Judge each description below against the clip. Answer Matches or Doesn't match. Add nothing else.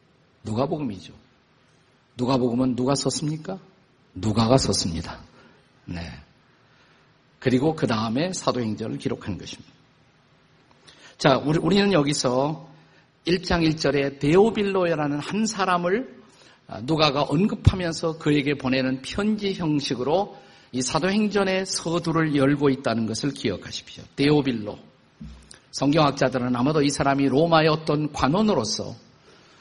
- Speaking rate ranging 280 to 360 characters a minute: Doesn't match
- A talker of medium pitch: Matches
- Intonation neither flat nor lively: Matches